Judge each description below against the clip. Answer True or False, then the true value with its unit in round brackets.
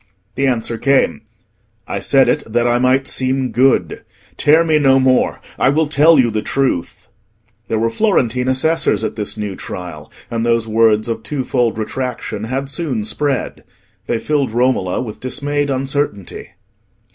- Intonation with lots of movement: False (3.5 semitones)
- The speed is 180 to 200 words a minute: False (155 wpm)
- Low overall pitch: True (130 Hz)